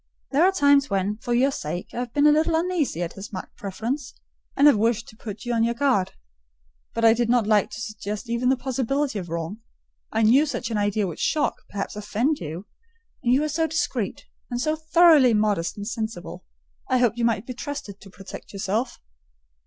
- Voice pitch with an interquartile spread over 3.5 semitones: Yes, average, 5.2 semitones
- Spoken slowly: No, fast, 205 wpm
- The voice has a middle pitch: No, high, 235 Hz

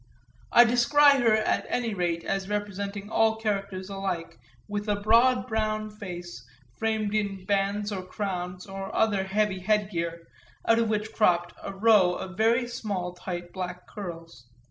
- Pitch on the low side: No, high, 200 Hz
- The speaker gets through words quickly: No, average, 150 wpm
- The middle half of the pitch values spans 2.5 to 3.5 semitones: Yes, average, 2.9 semitones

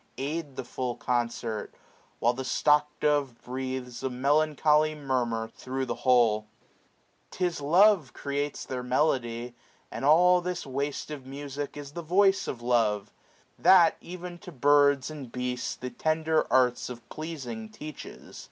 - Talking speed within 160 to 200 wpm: No, average, 145 wpm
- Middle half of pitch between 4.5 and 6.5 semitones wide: No, average, 3.8 semitones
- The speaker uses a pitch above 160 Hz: No, medium, 140 Hz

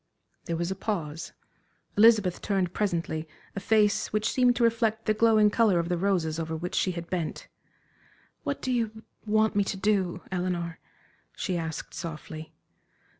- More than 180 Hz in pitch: Yes, high, 190 Hz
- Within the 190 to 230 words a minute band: No, average, 165 wpm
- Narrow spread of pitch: No, average, 4.2 semitones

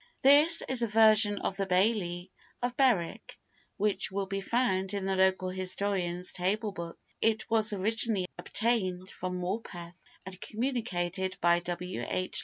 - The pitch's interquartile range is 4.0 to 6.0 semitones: No, average, 3.3 semitones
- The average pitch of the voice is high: Yes, high, 195 Hz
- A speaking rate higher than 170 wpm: No, average, 145 wpm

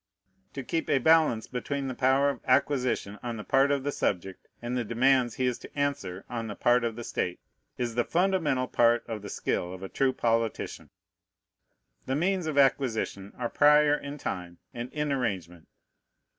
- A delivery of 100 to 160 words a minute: No, average, 185 wpm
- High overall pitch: No, low, 125 Hz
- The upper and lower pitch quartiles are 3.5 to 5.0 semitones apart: Yes, average, 3.9 semitones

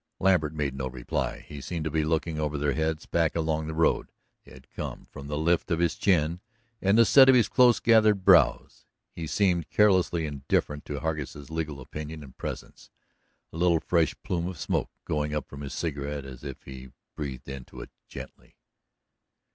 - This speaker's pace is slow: No, average, 185 wpm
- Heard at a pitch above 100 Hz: No, very low, 80 Hz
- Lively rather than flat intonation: No, average, 3.2 semitones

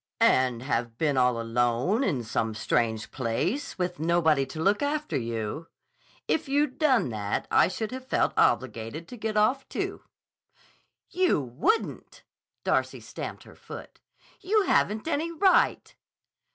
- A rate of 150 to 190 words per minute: No, slow, 135 wpm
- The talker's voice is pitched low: No, medium, 160 Hz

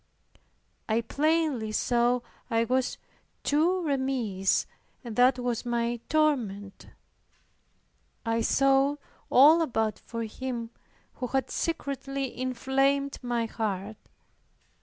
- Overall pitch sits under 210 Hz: No, very high, 250 Hz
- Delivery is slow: Yes, slow, 95 wpm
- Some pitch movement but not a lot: Yes, average, 3.2 semitones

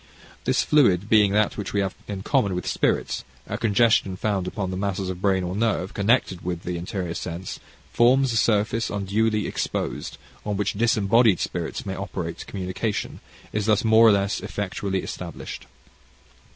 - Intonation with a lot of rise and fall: No, average, 2.7 semitones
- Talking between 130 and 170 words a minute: Yes, average, 165 wpm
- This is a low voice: Yes, low, 100 Hz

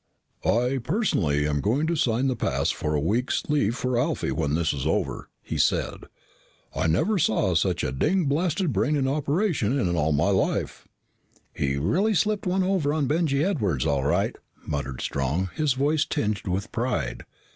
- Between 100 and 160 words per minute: No, average, 175 wpm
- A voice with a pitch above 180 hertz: No, low, 125 Hz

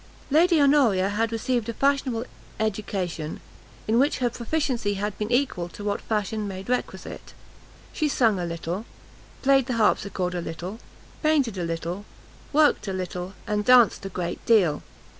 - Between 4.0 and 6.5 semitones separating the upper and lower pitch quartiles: Yes, average, 5.2 semitones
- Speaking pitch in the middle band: No, high, 215 Hz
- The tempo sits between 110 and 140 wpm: No, average, 155 wpm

